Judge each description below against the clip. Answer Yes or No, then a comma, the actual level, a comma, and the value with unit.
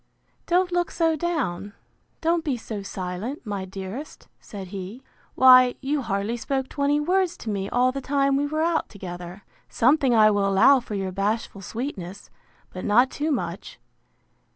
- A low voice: No, high, 245 Hz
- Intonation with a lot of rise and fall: Yes, wide, 6.6 semitones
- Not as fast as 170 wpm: Yes, average, 160 wpm